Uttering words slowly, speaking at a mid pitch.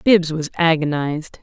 Yes: slow, 125 wpm; medium, 160 Hz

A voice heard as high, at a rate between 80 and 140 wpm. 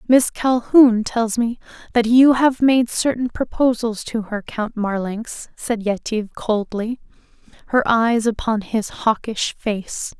Yes: high, 230 Hz; slow, 135 wpm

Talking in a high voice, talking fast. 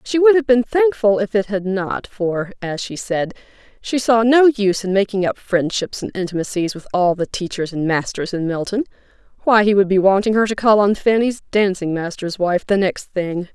Yes: high, 200 Hz; fast, 210 wpm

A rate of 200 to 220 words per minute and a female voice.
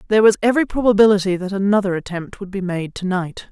Yes: fast, 205 wpm; female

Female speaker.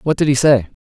No: male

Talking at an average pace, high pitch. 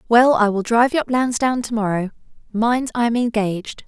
Yes: average, 185 wpm; high, 230 Hz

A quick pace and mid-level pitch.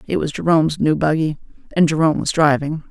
No: average, 185 wpm; medium, 155 Hz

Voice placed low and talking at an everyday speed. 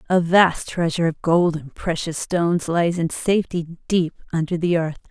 No: medium, 170 Hz; average, 175 wpm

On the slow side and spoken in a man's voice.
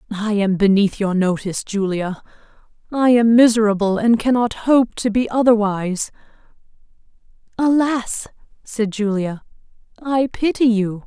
No: slow, 115 wpm; female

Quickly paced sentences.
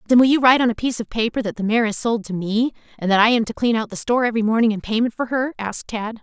Yes: fast, 320 wpm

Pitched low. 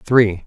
Yes: low, 105 Hz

